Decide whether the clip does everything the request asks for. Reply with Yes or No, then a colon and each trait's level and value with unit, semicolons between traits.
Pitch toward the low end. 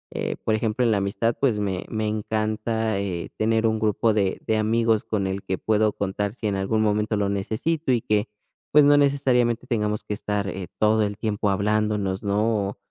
Yes: low, 110 Hz